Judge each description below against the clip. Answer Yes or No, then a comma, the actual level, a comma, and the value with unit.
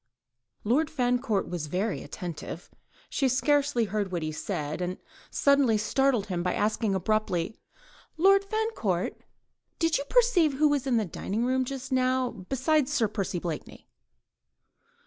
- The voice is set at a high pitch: Yes, high, 235 Hz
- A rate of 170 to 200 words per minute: No, average, 140 wpm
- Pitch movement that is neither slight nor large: No, wide, 6.6 semitones